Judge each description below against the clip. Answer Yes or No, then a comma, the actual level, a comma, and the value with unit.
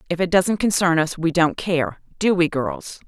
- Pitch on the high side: No, medium, 175 Hz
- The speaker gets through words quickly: Yes, fast, 215 wpm